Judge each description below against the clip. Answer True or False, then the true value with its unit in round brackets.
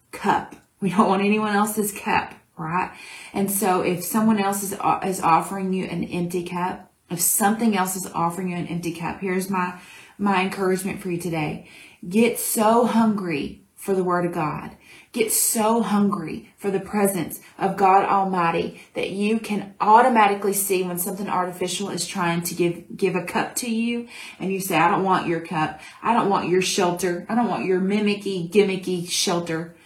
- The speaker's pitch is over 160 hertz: True (190 Hz)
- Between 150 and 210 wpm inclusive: True (180 wpm)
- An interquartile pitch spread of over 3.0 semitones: False (2.4 semitones)